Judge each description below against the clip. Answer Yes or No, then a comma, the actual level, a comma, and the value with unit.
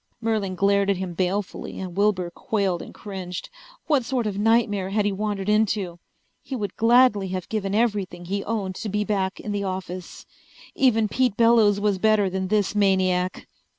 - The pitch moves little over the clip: Yes, narrow, 2.3 semitones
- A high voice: Yes, high, 200 Hz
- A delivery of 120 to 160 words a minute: No, average, 175 wpm